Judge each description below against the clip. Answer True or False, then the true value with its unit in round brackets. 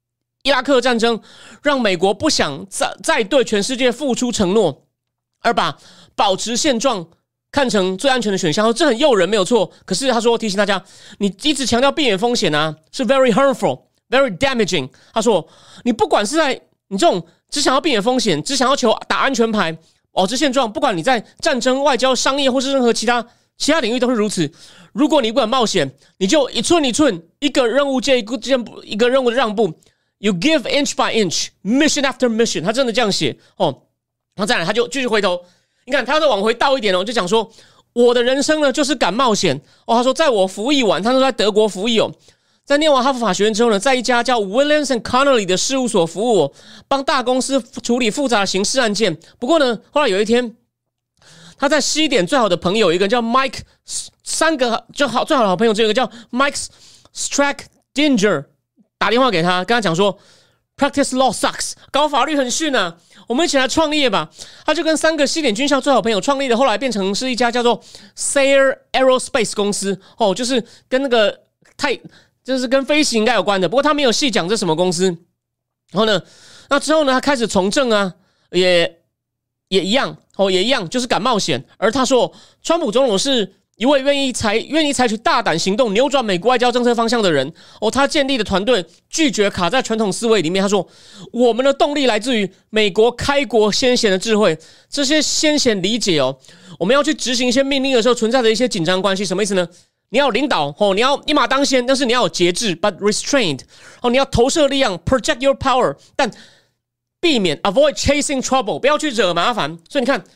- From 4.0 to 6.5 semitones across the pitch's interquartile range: True (5.4 semitones)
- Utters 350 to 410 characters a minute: True (370 characters per minute)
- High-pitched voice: True (240 Hz)